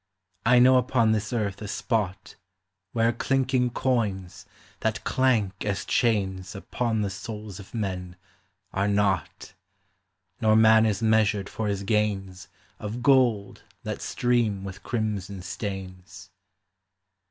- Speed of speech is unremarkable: No, slow, 120 wpm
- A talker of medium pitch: No, low, 105 Hz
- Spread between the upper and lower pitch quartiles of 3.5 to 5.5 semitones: No, average, 3.0 semitones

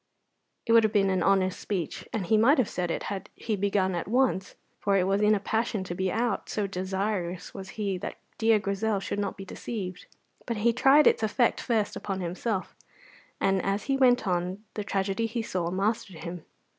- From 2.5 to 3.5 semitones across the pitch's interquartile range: Yes, average, 2.8 semitones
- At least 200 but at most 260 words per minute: Yes, fast, 205 wpm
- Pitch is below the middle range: No, high, 200 Hz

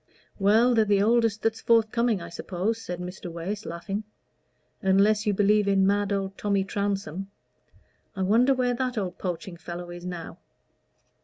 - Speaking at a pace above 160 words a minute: No, average, 155 wpm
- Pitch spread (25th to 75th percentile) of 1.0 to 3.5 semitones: Yes, average, 3.1 semitones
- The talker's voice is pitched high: Yes, high, 200 Hz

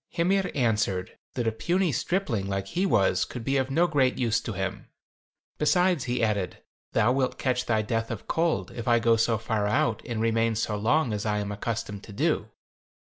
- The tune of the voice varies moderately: Yes, average, 4.2 semitones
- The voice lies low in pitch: Yes, low, 115 Hz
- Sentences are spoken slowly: No, average, 195 wpm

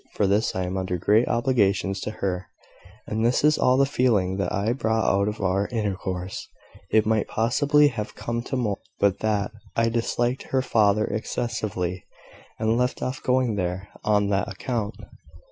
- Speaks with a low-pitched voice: Yes, low, 110 Hz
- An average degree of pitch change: Yes, average, 3.3 semitones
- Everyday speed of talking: Yes, average, 170 wpm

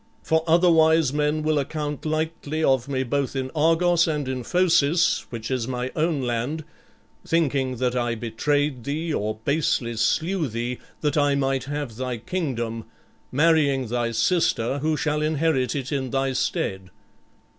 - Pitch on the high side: No, medium, 140 Hz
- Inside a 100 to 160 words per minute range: Yes, average, 150 wpm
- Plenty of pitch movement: No, average, 3.9 semitones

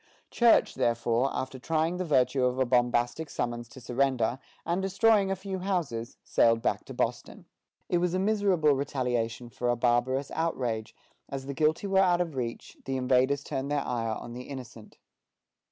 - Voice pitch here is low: Yes, low, 130 Hz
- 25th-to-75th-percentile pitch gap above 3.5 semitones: Yes, wide, 5.6 semitones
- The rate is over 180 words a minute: No, average, 170 wpm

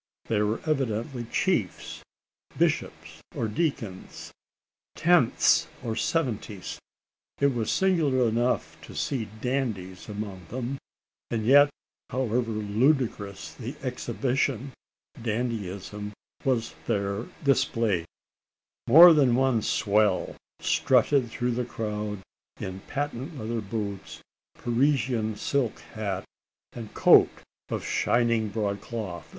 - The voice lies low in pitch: Yes, low, 115 Hz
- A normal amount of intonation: Yes, average, 3.9 semitones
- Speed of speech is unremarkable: No, slow, 100 wpm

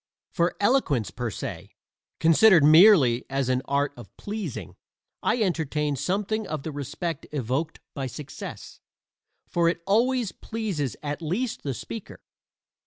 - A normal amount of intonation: No, wide, 6.6 semitones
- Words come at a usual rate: No, slow, 130 wpm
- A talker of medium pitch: Yes, medium, 160 Hz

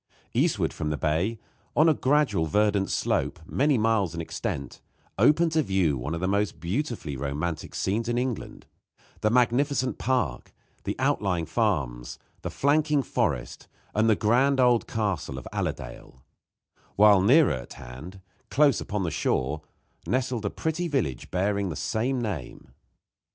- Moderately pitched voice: No, low, 105 Hz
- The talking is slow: No, average, 145 wpm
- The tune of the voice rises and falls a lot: Yes, wide, 7.9 semitones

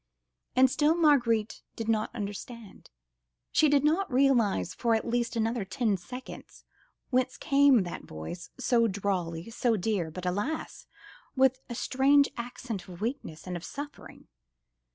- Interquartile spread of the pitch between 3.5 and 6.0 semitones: Yes, average, 4.8 semitones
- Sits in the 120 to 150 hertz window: No, high, 230 Hz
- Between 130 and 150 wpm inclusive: Yes, average, 140 wpm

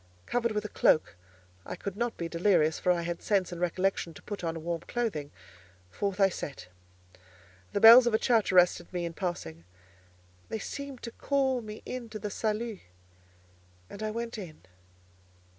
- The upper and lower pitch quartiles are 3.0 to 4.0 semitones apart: No, average, 4.9 semitones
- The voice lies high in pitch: Yes, high, 200 Hz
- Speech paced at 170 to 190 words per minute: Yes, average, 175 wpm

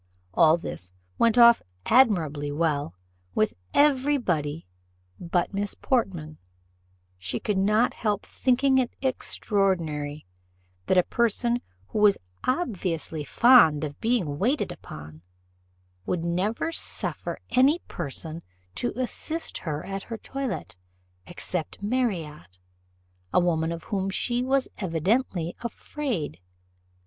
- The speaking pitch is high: Yes, high, 195 Hz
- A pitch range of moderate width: No, wide, 7.4 semitones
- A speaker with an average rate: No, slow, 115 wpm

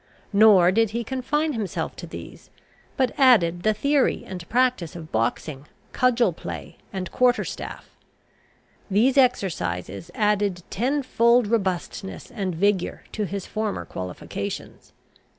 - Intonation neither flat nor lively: No, wide, 5.7 semitones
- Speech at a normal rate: No, slow, 125 wpm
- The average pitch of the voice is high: Yes, high, 210 Hz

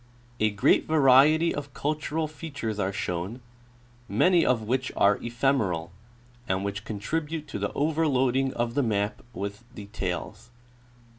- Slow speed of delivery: Yes, slow, 130 wpm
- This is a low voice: Yes, low, 125 Hz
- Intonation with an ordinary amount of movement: No, wide, 6.2 semitones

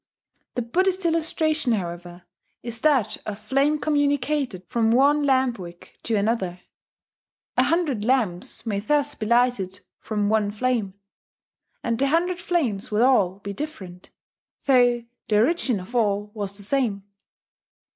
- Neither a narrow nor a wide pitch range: No, wide, 5.9 semitones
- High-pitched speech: Yes, high, 235 Hz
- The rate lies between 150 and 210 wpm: No, slow, 135 wpm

